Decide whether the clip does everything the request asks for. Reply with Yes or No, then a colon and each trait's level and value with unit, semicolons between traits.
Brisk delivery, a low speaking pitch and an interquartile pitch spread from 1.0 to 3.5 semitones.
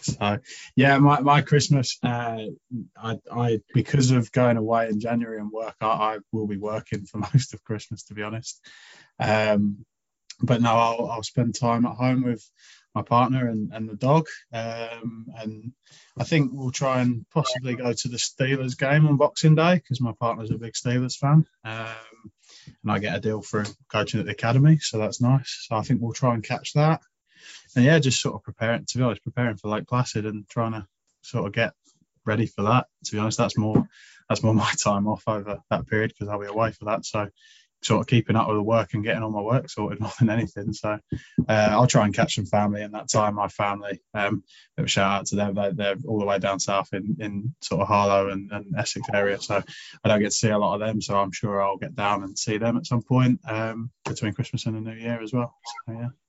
Yes: fast, 230 wpm; low, 115 Hz; average, 2.9 semitones